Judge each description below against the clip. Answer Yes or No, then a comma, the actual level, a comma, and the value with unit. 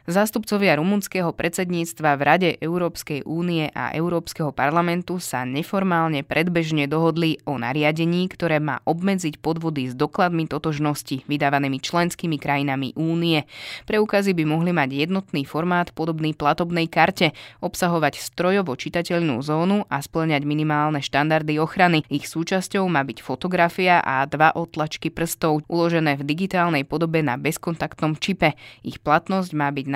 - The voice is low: No, medium, 160 Hz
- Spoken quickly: No, average, 130 wpm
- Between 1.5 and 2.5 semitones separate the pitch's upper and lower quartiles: No, average, 2.9 semitones